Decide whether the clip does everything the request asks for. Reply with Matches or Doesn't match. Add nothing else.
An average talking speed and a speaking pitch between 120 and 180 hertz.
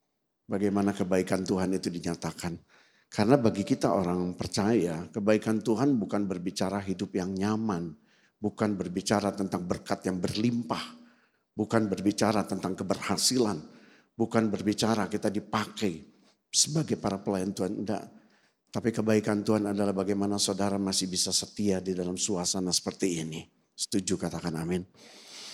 Doesn't match